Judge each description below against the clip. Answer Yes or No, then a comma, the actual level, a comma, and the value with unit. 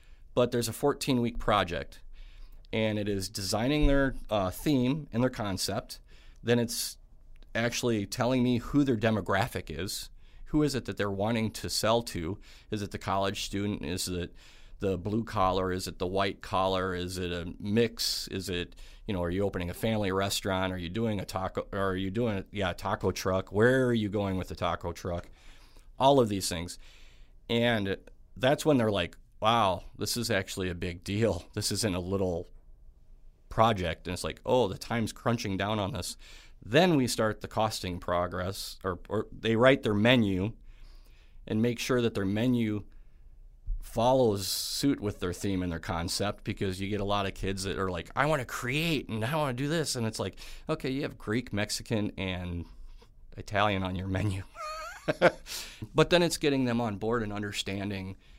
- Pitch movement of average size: Yes, average, 4.0 semitones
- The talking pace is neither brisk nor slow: Yes, average, 185 wpm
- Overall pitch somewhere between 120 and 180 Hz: No, low, 100 Hz